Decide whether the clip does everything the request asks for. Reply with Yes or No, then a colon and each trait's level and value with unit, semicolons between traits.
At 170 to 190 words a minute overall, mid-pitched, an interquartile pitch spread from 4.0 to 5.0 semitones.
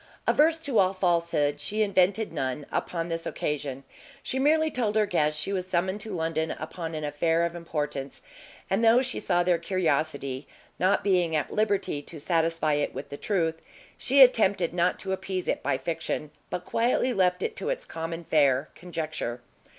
Yes: average, 175 wpm; medium, 170 Hz; average, 4.3 semitones